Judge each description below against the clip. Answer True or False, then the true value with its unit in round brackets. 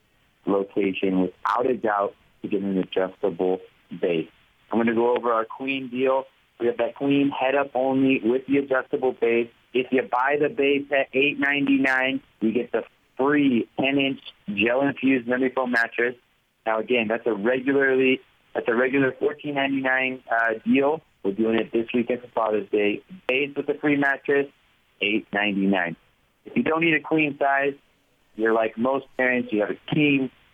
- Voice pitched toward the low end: True (130 Hz)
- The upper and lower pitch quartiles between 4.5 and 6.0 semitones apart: False (3.4 semitones)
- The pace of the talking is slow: False (170 wpm)